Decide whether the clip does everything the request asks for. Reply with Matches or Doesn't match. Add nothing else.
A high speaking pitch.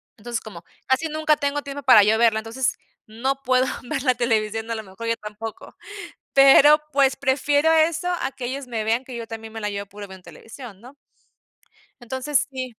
Matches